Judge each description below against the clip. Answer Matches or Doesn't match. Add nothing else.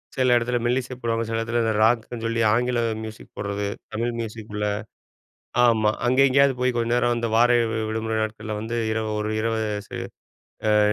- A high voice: Doesn't match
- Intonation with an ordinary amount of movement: Doesn't match